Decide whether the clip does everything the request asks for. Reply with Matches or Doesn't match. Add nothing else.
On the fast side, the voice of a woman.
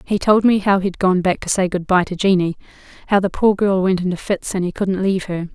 Matches